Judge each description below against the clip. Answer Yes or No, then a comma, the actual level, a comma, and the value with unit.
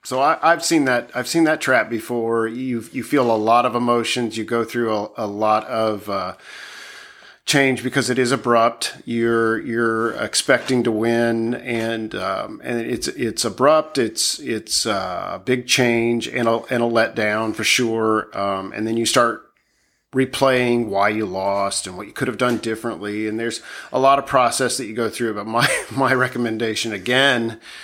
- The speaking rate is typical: Yes, average, 180 wpm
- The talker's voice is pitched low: Yes, low, 115 Hz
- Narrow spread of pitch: Yes, narrow, 2.1 semitones